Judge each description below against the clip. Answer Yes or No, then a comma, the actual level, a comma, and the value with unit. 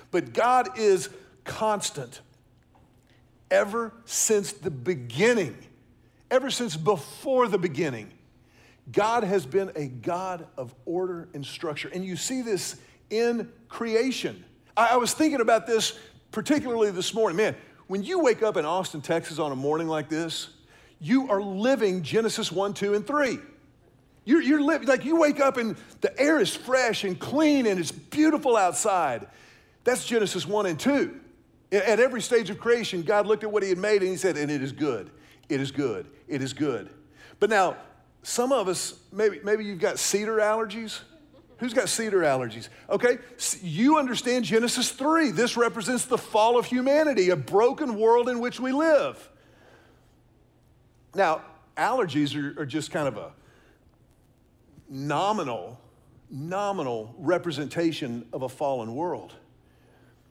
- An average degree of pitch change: No, wide, 7.9 semitones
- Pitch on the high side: Yes, high, 200 Hz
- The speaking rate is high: No, average, 155 wpm